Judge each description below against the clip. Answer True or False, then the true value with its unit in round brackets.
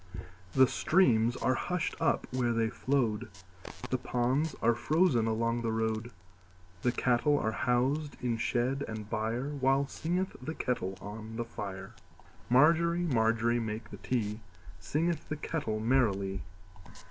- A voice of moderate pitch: False (120 Hz)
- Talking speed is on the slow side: True (120 wpm)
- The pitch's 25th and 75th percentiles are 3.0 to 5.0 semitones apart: True (3.7 semitones)